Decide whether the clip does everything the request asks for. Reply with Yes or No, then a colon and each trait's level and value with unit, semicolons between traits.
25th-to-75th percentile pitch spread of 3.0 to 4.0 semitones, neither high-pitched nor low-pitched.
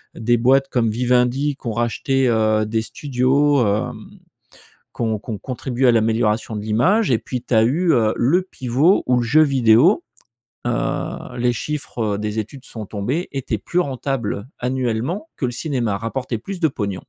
No: average, 3.6 semitones; low, 125 Hz